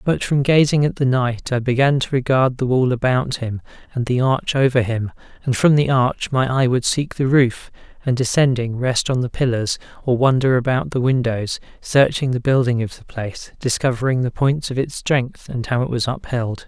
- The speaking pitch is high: No, low, 130 Hz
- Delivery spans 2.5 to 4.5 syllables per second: No, 5.0 syllables/s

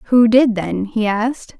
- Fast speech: No, average, 190 wpm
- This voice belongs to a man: No, female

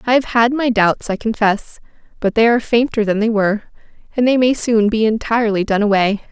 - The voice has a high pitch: Yes, high, 220 Hz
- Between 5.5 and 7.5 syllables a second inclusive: Yes, 5.7 syllables/s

